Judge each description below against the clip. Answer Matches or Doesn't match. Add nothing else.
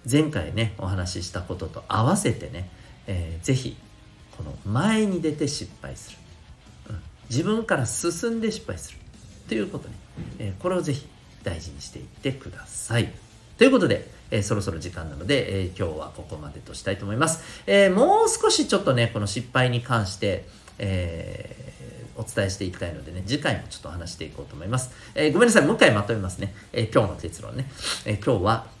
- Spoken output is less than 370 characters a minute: Matches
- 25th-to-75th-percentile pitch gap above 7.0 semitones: Doesn't match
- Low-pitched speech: Matches